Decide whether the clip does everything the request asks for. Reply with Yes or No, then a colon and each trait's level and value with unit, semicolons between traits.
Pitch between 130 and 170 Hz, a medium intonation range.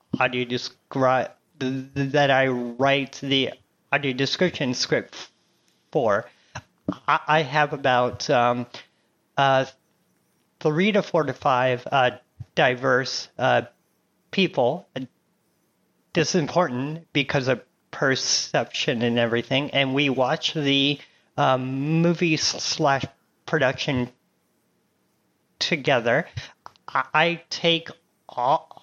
Yes: medium, 140 Hz; average, 3.5 semitones